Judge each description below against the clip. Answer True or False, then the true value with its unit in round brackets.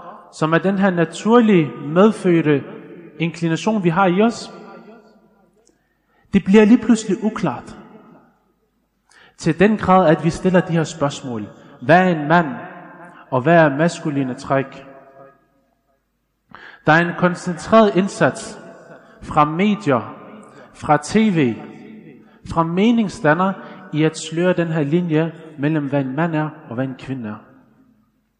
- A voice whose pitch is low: False (170 Hz)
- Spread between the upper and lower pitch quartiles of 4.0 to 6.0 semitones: True (4.5 semitones)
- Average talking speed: False (130 wpm)